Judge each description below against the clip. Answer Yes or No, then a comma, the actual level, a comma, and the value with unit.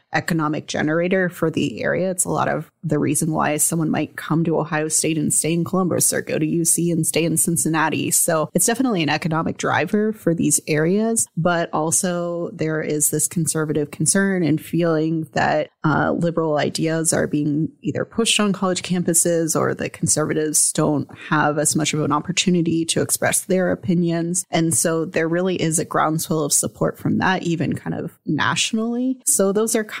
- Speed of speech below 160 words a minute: No, average, 185 wpm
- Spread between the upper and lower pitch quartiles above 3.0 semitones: No, narrow, 2.4 semitones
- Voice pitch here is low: No, medium, 165 Hz